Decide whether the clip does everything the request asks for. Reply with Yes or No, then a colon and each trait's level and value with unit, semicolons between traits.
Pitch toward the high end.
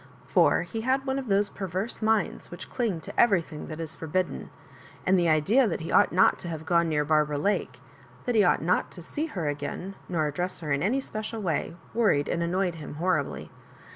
No: medium, 180 Hz